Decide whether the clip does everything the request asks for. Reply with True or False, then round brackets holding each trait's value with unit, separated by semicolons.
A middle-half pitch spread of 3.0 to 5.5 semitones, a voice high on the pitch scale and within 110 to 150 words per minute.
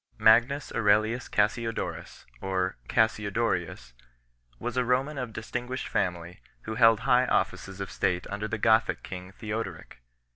False (3.9 semitones; 110 Hz; 135 wpm)